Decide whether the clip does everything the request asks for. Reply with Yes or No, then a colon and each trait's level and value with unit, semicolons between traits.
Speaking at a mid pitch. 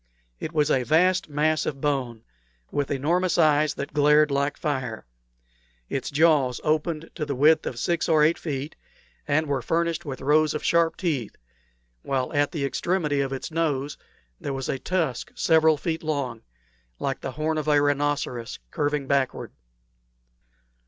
Yes: medium, 150 Hz